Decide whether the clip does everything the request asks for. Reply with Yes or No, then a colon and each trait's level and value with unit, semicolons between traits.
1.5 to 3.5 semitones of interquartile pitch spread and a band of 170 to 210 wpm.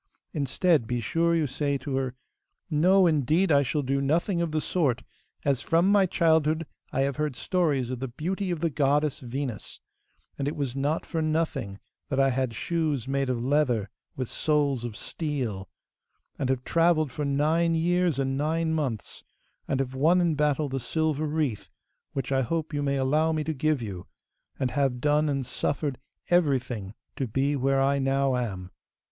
Yes: average, 3.2 semitones; average, 180 wpm